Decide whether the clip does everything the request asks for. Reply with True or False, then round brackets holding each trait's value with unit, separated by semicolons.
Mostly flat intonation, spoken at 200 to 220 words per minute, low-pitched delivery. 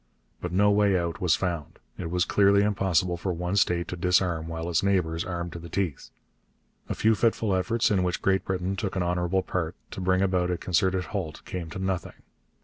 True (1.9 semitones; 205 wpm; 90 Hz)